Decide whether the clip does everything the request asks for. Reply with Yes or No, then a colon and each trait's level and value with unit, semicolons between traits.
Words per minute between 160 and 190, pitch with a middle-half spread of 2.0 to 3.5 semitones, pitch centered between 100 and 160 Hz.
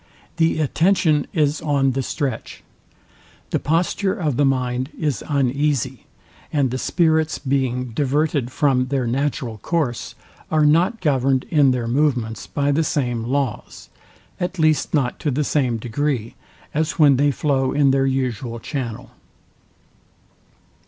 No: slow, 135 wpm; average, 3.0 semitones; medium, 140 Hz